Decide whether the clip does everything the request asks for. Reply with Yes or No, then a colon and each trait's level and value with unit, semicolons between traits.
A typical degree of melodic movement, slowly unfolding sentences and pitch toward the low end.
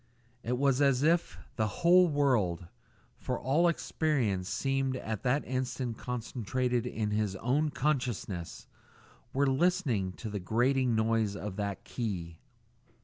Yes: average, 4.6 semitones; slow, 130 wpm; low, 125 Hz